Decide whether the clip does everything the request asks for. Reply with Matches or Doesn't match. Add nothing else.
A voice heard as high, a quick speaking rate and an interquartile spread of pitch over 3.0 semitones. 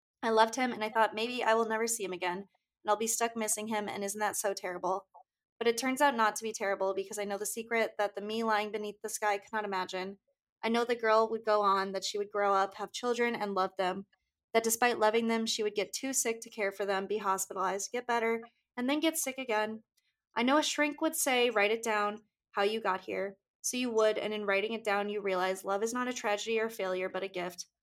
Doesn't match